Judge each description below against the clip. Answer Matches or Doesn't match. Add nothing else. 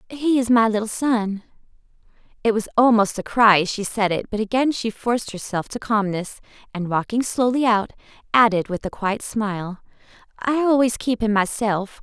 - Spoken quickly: Doesn't match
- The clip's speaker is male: Doesn't match